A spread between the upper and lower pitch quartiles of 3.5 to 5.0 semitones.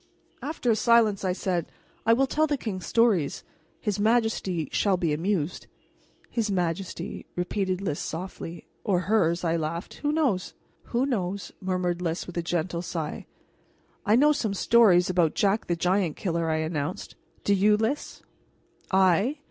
Yes: average, 4.2 semitones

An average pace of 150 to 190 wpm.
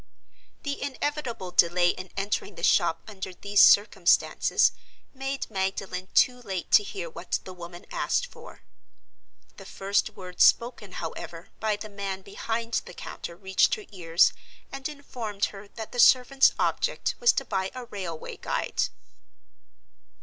No: average, 140 wpm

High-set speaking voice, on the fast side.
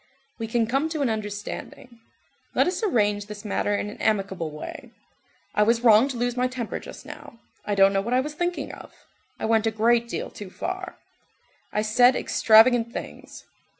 No: high, 225 Hz; average, 185 wpm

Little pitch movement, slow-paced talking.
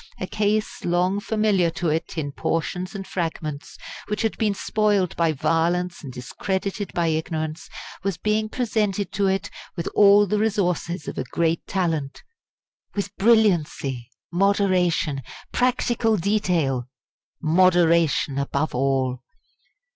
No: average, 4.3 semitones; slow, 125 wpm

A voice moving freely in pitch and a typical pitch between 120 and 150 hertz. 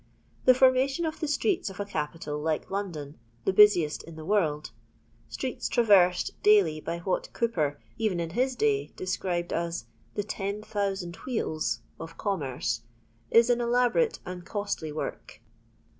No: wide, 6.5 semitones; high, 190 Hz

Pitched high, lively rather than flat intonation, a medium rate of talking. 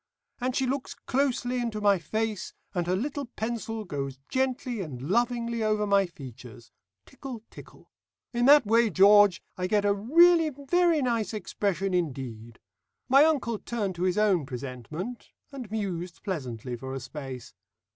Yes: high, 210 Hz; wide, 6.4 semitones; average, 150 wpm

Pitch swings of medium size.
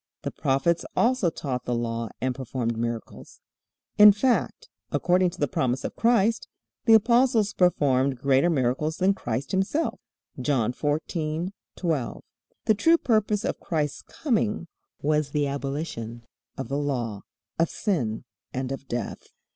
No: wide, 7.5 semitones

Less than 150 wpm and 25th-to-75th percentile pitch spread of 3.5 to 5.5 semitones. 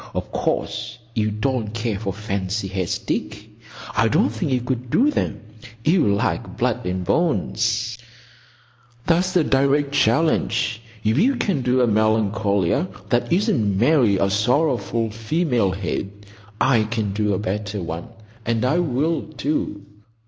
Yes: average, 140 wpm; average, 5.2 semitones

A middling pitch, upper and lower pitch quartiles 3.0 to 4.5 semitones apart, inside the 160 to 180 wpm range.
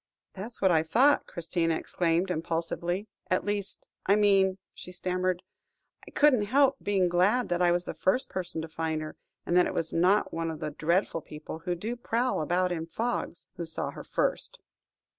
No: medium, 180 Hz; average, 3.6 semitones; average, 190 wpm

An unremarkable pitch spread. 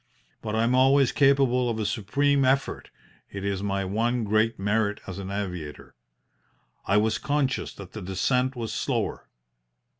Yes: average, 4.5 semitones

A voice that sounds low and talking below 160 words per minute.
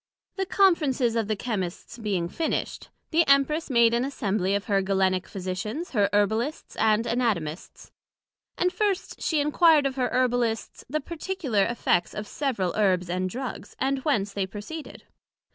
No: high, 230 Hz; average, 150 wpm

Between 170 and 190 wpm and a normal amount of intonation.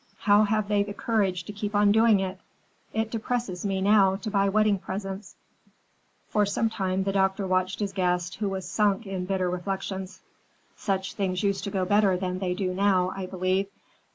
No: average, 185 wpm; narrow, 1.7 semitones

